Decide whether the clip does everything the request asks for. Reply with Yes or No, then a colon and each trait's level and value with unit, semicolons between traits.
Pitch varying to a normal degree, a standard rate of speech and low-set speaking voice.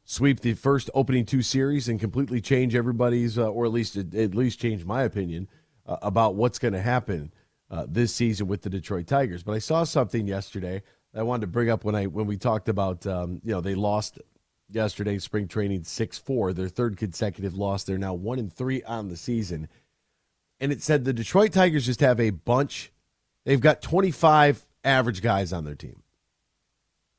Yes: average, 4.3 semitones; average, 195 wpm; low, 115 Hz